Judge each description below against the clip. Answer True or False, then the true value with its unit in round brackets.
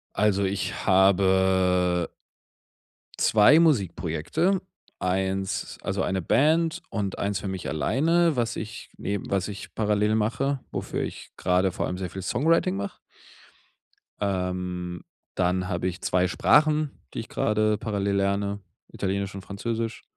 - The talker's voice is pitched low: True (100 Hz)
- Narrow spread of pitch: False (3.1 semitones)